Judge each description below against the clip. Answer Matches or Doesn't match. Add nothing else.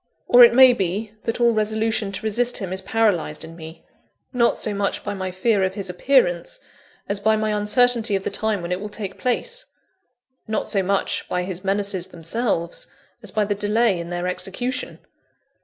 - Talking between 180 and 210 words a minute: Matches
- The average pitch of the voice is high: Matches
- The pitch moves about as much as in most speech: Matches